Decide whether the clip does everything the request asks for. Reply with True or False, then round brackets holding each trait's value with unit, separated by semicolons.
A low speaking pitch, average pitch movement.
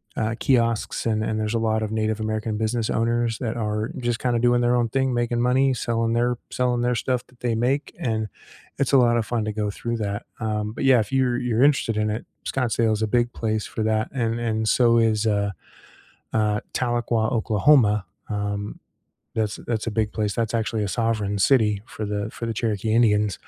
False (115 Hz; 2.0 semitones)